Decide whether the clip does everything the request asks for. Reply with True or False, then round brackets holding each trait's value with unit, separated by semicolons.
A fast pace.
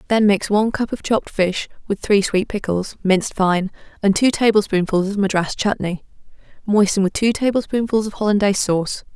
False (170 wpm)